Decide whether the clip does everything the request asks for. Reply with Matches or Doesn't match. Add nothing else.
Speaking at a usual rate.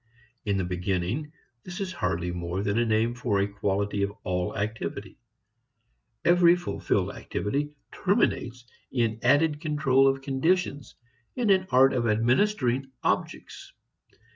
Doesn't match